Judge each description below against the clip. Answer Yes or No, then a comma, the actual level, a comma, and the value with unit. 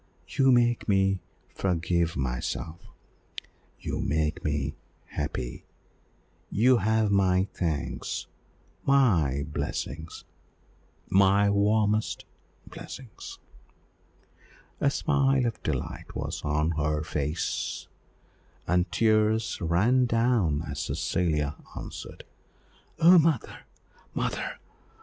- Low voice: Yes, very low, 95 Hz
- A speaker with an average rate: No, slow, 90 wpm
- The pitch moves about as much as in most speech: No, wide, 6.8 semitones